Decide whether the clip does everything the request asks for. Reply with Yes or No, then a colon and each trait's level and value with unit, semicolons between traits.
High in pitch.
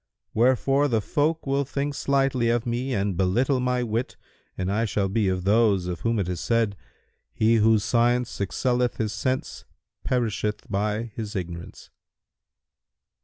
No: low, 115 Hz